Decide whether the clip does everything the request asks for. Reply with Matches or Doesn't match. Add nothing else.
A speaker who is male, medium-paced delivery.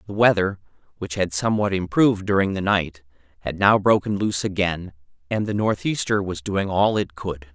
Matches